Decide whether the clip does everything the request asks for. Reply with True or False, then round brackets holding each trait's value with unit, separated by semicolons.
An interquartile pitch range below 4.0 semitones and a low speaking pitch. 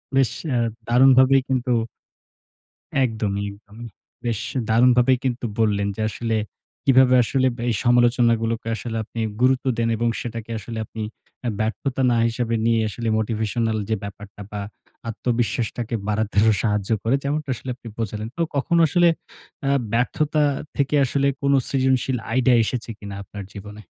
True (2.8 semitones; 120 Hz)